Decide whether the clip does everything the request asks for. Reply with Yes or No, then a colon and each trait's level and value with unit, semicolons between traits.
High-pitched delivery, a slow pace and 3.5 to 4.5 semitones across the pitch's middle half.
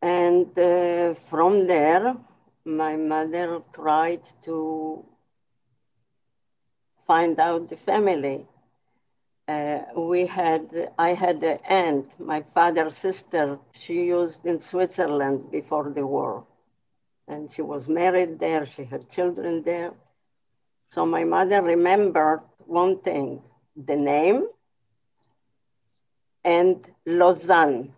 No: medium, 160 Hz; slow, 105 wpm; average, 4.0 semitones